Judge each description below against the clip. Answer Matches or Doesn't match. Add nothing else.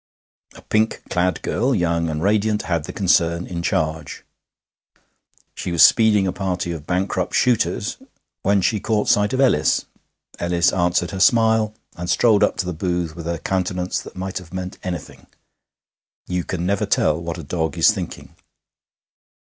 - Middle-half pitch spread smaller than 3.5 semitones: Matches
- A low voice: Matches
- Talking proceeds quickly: Doesn't match